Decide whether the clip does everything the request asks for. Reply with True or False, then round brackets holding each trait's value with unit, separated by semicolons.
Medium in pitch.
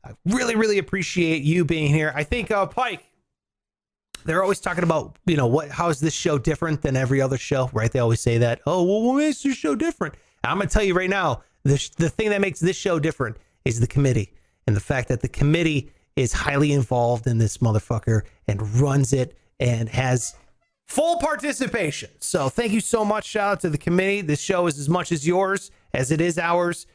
True (160 Hz)